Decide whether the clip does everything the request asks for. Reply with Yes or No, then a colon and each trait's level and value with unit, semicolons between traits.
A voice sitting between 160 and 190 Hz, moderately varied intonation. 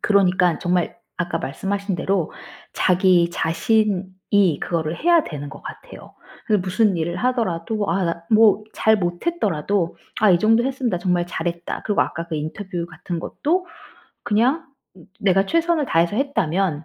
Yes: medium, 185 Hz; average, 4.1 semitones